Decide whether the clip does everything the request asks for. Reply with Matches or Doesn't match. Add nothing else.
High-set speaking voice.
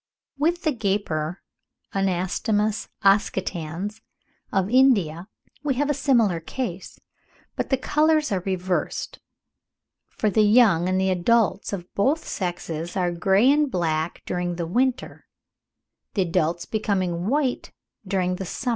Matches